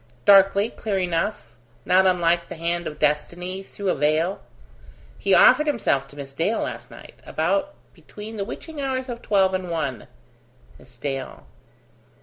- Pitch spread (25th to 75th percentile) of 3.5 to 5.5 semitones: Yes, average, 4.2 semitones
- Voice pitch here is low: No, medium, 185 Hz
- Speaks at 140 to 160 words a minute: Yes, average, 150 wpm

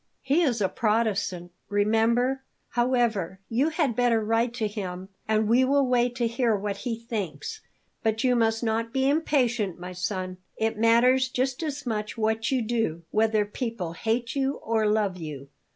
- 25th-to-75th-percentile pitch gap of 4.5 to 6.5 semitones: No, average, 3.0 semitones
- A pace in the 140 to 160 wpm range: No, average, 170 wpm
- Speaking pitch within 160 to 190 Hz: No, high, 225 Hz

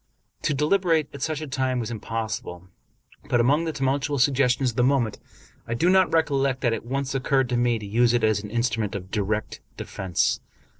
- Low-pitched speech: Yes, low, 125 Hz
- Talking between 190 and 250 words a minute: Yes, average, 195 wpm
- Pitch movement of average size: Yes, average, 3.8 semitones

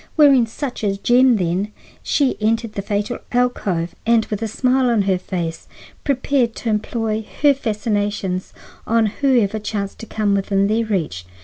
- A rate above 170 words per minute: No, average, 155 wpm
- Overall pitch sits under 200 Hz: No, high, 220 Hz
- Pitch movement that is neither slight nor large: Yes, average, 3.4 semitones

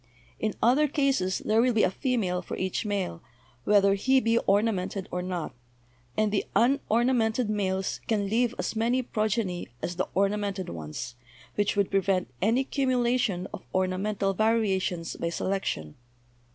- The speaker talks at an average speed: Yes, average, 150 wpm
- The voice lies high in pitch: Yes, high, 205 Hz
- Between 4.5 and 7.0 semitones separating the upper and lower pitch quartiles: No, average, 3.6 semitones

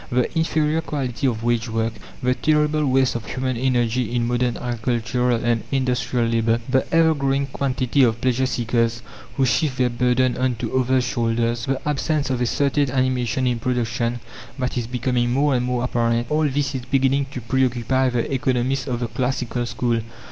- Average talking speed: Yes, average, 175 wpm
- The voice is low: Yes, low, 125 Hz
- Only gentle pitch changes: Yes, narrow, 2.1 semitones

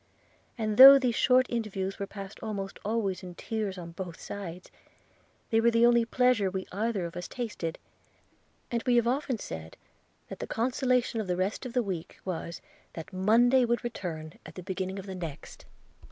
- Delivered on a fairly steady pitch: No, average, 4.4 semitones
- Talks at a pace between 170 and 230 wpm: Yes, average, 180 wpm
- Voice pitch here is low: No, high, 205 Hz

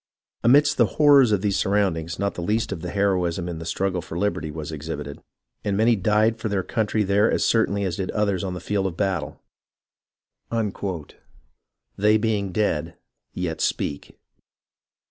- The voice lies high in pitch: No, low, 100 Hz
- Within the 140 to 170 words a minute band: Yes, average, 165 wpm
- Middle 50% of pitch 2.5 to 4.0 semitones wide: Yes, average, 3.5 semitones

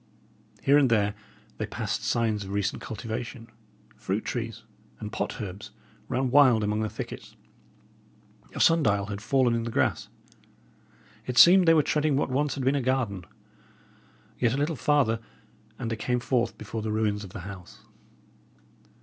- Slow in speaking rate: No, average, 165 wpm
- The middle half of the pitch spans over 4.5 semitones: No, average, 4.1 semitones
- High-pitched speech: No, low, 115 Hz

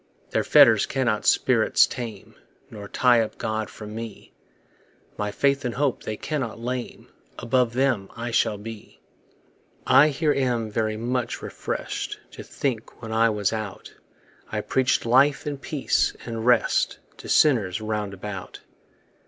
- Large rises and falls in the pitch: No, average, 3.1 semitones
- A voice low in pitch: Yes, low, 115 Hz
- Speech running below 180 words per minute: Yes, average, 145 wpm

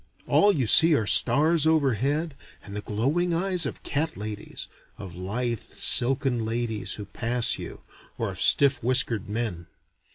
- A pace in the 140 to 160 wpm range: Yes, average, 150 wpm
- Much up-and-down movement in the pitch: Yes, wide, 6.1 semitones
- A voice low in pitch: Yes, low, 125 Hz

